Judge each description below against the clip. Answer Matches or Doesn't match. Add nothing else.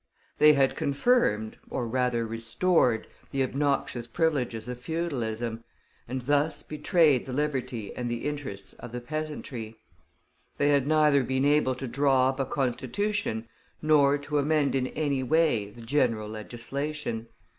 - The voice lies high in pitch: Doesn't match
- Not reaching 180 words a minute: Matches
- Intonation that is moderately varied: Matches